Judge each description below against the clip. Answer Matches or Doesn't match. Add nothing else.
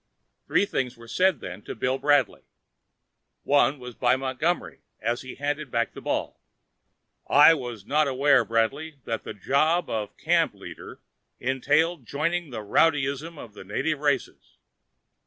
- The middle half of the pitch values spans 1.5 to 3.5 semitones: Doesn't match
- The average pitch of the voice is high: Doesn't match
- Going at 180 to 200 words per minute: Doesn't match